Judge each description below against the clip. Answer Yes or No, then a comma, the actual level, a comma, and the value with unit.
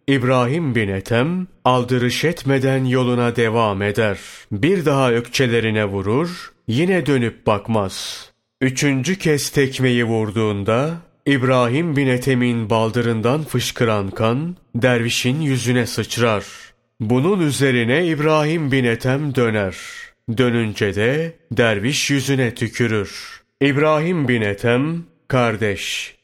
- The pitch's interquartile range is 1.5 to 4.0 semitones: Yes, average, 3.5 semitones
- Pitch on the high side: No, low, 125 Hz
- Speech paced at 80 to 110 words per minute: Yes, average, 100 wpm